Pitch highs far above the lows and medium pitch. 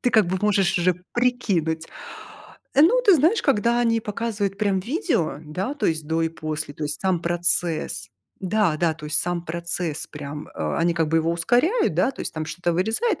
Yes: wide, 5.9 semitones; medium, 180 Hz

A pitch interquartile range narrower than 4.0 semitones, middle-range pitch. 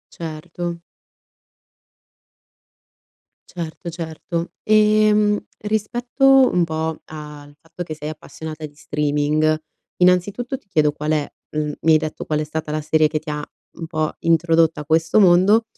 Yes: average, 2.8 semitones; medium, 160 Hz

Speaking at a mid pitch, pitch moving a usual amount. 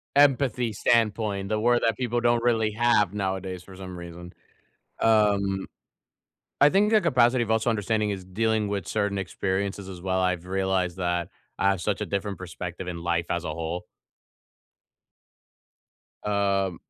No: low, 100 Hz; average, 3.3 semitones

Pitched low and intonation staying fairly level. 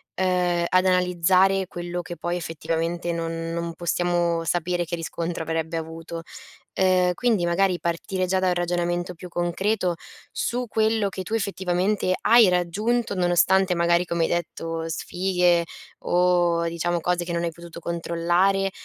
No: medium, 175 Hz; narrow, 1.5 semitones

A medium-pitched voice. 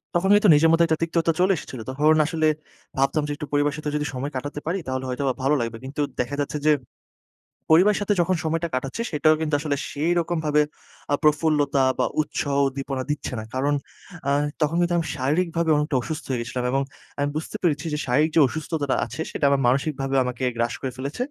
Yes: medium, 150 Hz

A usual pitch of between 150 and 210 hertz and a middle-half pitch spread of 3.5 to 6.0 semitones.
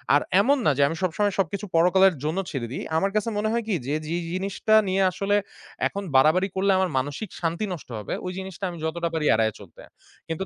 Yes: medium, 185 Hz; average, 3.8 semitones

